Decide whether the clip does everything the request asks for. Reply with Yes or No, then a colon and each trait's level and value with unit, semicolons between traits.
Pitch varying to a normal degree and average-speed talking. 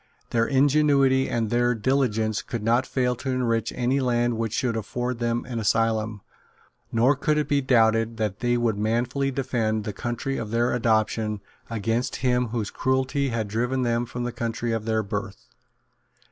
No: narrow, 2.3 semitones; average, 170 wpm